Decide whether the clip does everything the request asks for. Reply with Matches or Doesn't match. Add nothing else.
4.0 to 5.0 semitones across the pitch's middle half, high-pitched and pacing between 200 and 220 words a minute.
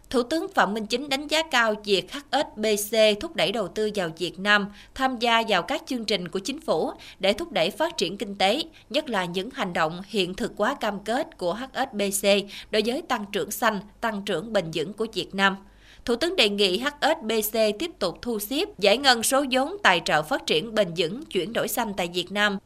Matches